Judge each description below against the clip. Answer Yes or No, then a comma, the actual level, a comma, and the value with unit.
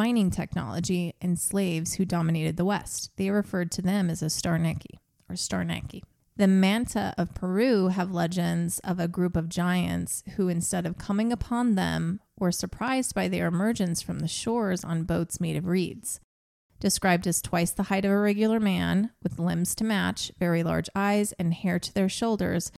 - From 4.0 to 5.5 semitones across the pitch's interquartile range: No, average, 2.7 semitones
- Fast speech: No, average, 180 wpm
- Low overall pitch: No, medium, 180 Hz